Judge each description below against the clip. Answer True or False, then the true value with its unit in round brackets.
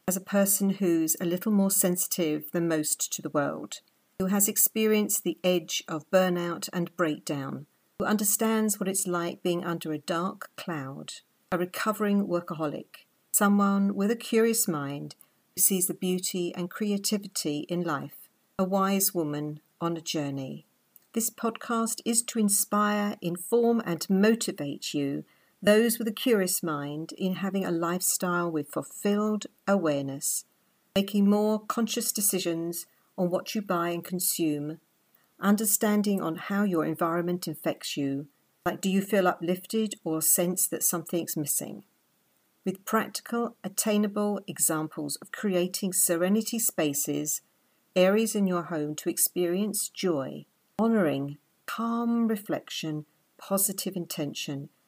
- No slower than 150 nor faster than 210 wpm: False (135 wpm)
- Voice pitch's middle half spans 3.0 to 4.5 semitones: True (3.8 semitones)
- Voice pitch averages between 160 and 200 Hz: True (185 Hz)